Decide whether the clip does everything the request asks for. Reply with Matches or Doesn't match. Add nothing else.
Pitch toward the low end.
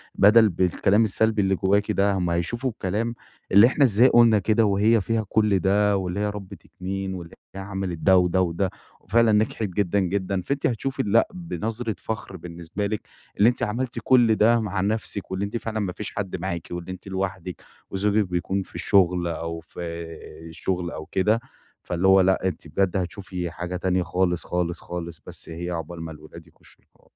Matches